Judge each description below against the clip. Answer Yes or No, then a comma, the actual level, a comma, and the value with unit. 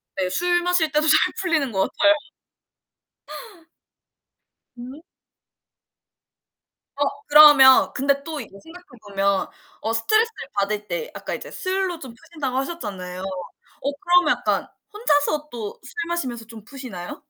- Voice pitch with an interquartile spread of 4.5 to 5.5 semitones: No, wide, 7.0 semitones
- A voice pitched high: Yes, very high, 280 Hz